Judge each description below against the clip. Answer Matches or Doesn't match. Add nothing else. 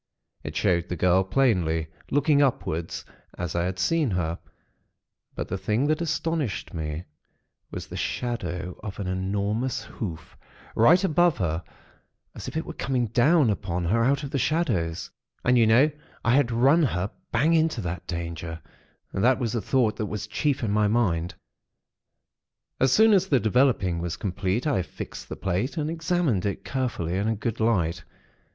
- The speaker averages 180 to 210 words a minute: Doesn't match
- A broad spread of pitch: Matches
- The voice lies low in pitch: Matches